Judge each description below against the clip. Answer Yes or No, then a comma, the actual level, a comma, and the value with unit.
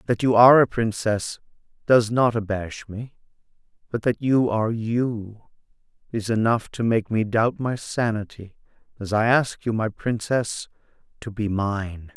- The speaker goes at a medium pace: Yes, average, 155 wpm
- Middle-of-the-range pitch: No, low, 110 Hz